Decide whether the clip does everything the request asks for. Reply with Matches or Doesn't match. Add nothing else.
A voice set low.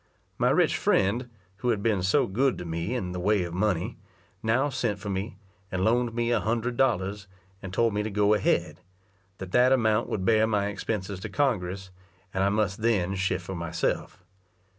Matches